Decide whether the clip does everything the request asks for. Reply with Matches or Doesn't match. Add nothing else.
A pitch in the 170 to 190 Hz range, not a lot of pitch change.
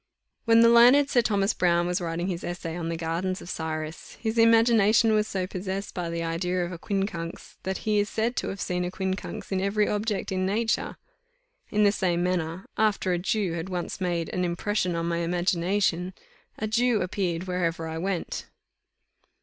Doesn't match